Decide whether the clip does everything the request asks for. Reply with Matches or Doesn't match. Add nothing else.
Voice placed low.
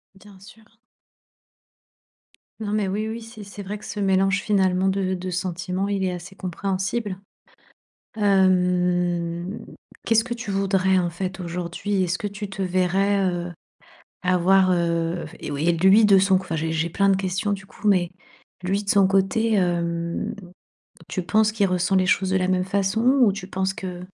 Doesn't match